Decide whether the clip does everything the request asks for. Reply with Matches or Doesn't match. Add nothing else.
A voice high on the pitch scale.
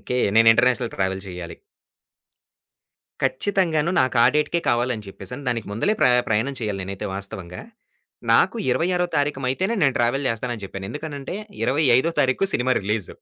Doesn't match